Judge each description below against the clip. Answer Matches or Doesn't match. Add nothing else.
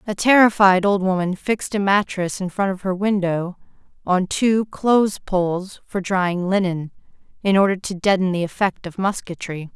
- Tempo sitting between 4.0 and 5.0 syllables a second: Matches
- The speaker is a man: Doesn't match